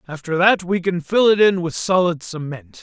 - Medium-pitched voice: Yes, medium, 175 Hz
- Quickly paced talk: Yes, fast, 215 wpm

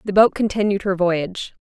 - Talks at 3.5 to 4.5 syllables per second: No, 5.5 syllables/s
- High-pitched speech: Yes, high, 195 Hz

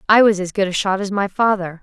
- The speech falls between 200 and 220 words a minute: No, fast, 295 wpm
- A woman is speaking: Yes, female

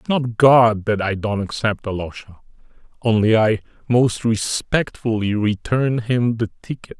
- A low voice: Yes, low, 110 Hz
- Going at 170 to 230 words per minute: No, slow, 135 wpm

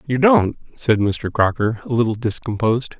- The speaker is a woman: No, male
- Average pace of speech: Yes, average, 160 wpm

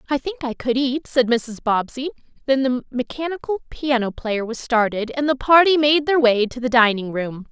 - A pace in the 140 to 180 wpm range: No, average, 200 wpm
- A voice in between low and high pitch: No, very high, 255 Hz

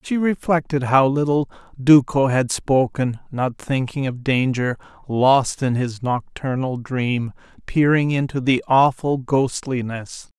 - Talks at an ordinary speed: No, slow, 120 wpm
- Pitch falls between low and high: No, low, 130 Hz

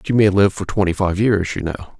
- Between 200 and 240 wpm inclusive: No, fast, 300 wpm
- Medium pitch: No, very low, 95 Hz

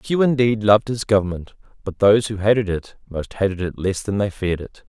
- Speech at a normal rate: No, fast, 220 wpm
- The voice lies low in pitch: Yes, low, 105 Hz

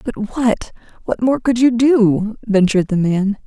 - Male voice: No, female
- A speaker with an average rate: Yes, average, 155 wpm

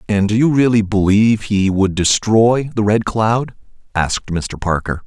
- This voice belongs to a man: Yes, male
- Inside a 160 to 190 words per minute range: Yes, average, 165 wpm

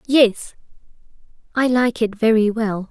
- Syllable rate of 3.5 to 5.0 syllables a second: Yes, 4.0 syllables/s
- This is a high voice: Yes, high, 225 Hz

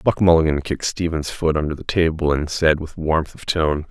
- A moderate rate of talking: No, fast, 215 wpm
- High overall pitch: No, very low, 80 Hz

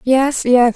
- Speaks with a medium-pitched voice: No, very high, 255 Hz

